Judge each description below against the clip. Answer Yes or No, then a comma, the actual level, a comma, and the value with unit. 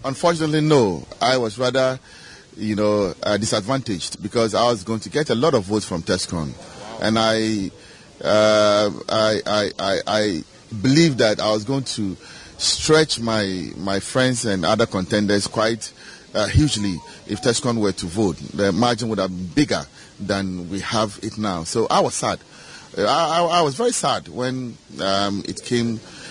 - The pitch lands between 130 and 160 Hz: No, low, 110 Hz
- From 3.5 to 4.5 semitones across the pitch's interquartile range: Yes, average, 3.9 semitones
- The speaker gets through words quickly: No, average, 170 wpm